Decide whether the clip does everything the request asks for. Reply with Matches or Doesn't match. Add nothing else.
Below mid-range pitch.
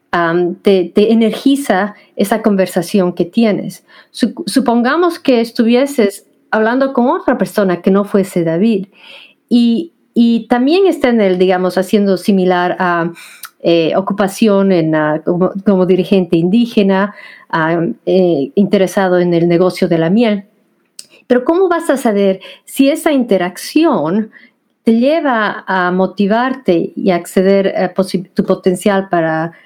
Doesn't match